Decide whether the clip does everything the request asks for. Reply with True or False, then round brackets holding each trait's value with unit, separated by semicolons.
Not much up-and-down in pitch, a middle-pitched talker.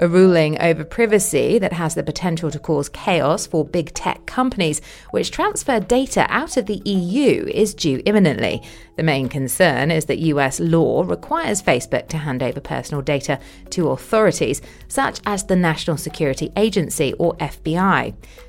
False (5.3 semitones; 165 Hz)